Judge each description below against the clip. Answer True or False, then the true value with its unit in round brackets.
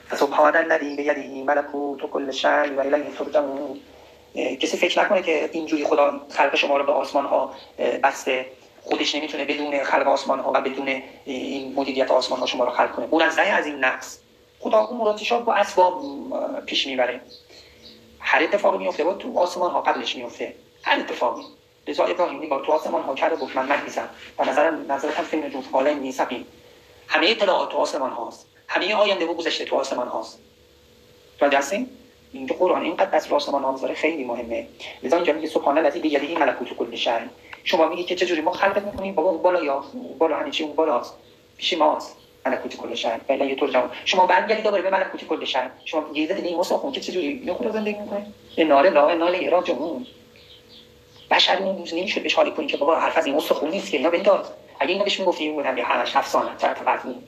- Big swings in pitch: True (6.0 semitones)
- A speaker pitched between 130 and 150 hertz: False (170 Hz)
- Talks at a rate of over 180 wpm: False (170 wpm)